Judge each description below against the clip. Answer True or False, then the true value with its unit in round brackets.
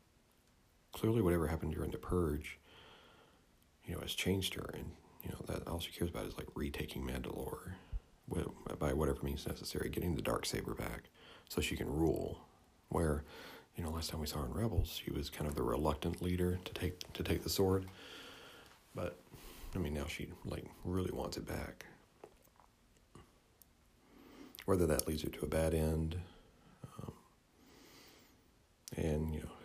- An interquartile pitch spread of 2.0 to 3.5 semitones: True (2.9 semitones)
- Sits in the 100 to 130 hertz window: False (85 Hz)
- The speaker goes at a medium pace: True (165 wpm)